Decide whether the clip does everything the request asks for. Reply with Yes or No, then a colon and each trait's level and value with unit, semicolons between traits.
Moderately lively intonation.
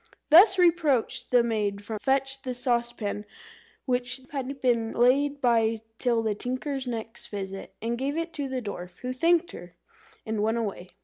Yes: average, 3.5 semitones